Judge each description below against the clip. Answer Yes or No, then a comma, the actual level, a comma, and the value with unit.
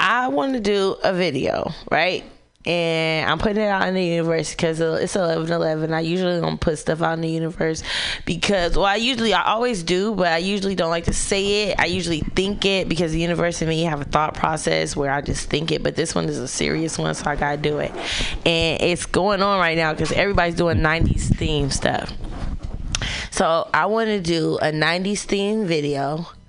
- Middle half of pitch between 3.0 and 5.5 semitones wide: Yes, average, 3.4 semitones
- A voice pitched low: No, medium, 170 Hz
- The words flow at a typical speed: No, fast, 215 wpm